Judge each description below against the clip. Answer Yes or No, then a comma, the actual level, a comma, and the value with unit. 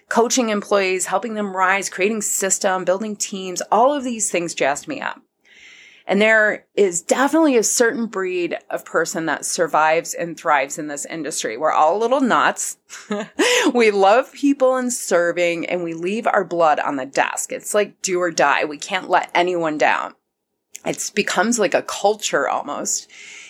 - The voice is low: No, high, 200 Hz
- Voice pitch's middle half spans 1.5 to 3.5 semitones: No, average, 4.3 semitones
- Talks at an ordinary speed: Yes, average, 170 wpm